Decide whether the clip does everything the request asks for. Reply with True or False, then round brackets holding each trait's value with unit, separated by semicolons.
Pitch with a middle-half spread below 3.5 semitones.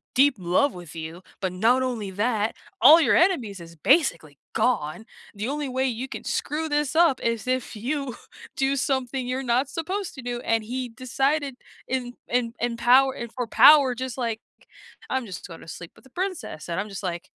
False (4.0 semitones)